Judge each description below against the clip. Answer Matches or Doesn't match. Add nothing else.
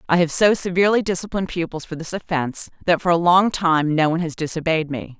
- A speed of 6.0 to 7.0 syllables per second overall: Matches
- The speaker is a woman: Matches